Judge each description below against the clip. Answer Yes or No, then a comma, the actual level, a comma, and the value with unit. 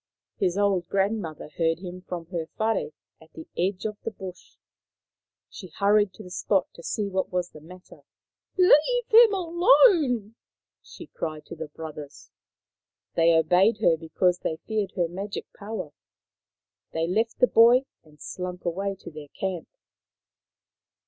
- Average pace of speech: Yes, average, 155 wpm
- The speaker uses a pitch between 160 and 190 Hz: Yes, medium, 185 Hz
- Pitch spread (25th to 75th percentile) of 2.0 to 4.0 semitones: No, average, 4.5 semitones